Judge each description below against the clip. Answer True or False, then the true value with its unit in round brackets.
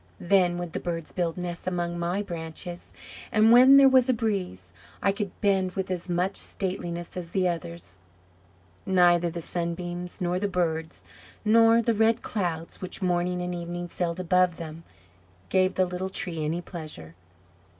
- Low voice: False (180 Hz)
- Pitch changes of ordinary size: False (2.0 semitones)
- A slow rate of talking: False (160 wpm)